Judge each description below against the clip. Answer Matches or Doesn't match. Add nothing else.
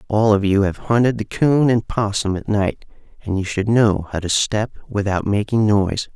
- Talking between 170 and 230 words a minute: Matches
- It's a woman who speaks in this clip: Doesn't match